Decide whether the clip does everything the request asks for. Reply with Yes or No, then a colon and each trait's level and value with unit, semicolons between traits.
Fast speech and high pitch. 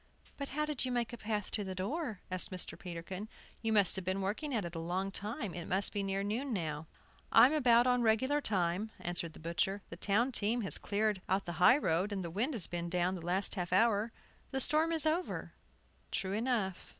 Yes: fast, 220 wpm; high, 205 Hz